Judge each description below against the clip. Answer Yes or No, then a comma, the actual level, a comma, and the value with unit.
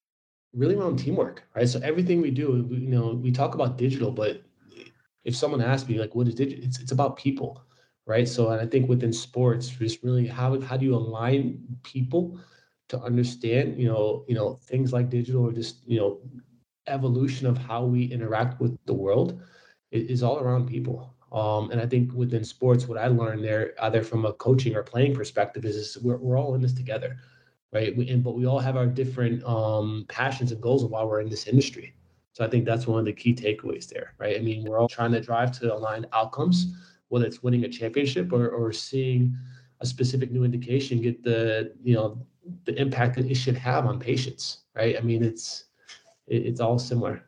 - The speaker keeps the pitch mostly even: Yes, narrow, 2.0 semitones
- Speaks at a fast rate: Yes, fast, 210 wpm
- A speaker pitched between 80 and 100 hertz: No, low, 125 Hz